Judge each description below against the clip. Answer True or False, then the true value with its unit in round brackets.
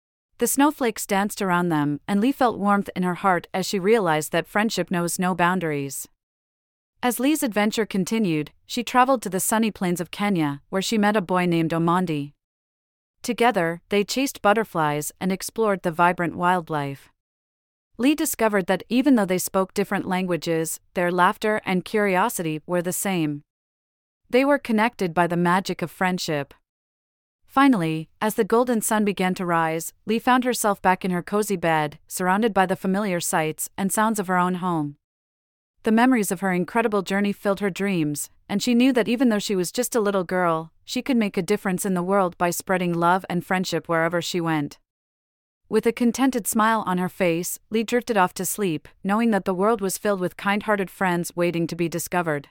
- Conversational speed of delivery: True (185 wpm)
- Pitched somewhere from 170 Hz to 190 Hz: True (185 Hz)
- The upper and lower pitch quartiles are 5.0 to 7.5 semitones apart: False (4.1 semitones)